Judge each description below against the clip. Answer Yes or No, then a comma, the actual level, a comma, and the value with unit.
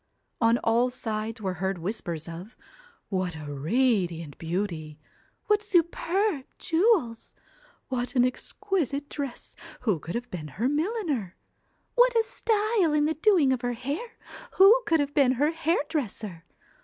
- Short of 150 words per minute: Yes, average, 140 wpm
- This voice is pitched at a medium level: No, very high, 250 Hz